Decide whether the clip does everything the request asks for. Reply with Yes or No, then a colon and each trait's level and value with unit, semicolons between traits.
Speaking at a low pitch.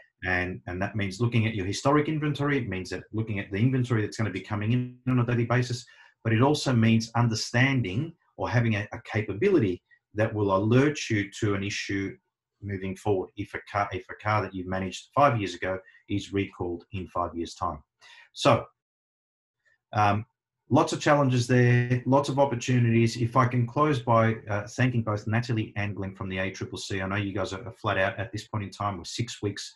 Yes: low, 110 Hz